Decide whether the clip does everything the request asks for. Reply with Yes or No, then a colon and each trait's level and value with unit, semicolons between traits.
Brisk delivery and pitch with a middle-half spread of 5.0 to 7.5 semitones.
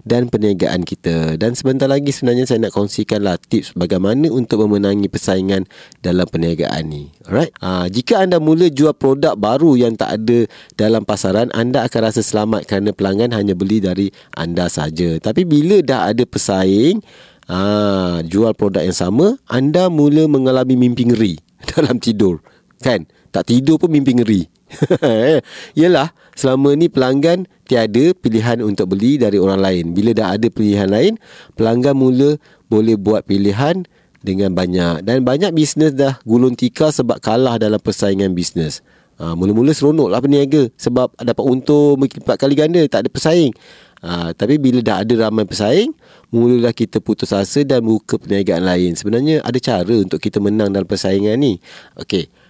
Yes: fast, 160 wpm; wide, 5.4 semitones